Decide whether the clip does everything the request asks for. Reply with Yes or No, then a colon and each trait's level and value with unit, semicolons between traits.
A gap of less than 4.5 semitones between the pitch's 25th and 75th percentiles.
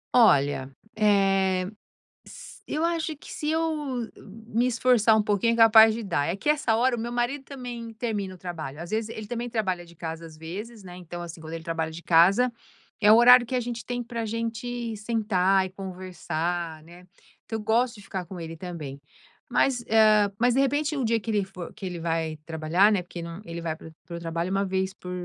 No: wide, 5.4 semitones